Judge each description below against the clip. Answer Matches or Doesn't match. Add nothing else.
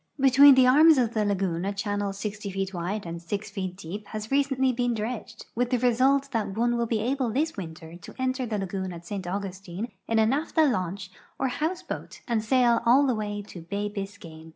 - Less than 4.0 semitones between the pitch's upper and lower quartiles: Doesn't match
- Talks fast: Matches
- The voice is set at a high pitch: Matches